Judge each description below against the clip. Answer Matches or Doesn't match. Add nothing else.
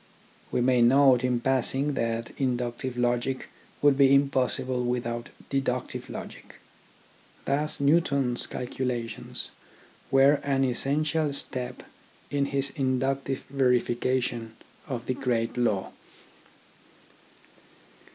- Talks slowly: Matches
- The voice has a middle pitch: Doesn't match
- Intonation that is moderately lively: Doesn't match